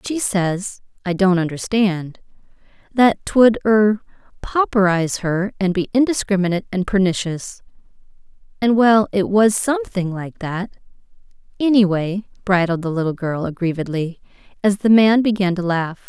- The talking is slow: Yes, slow, 115 wpm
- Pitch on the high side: Yes, high, 195 Hz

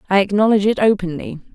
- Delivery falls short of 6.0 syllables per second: No, 7.3 syllables/s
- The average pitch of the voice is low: No, high, 200 Hz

